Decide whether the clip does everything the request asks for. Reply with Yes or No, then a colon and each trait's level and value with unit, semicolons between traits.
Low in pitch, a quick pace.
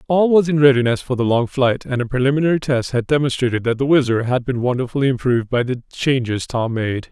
Yes: low, 130 Hz; fast, 220 wpm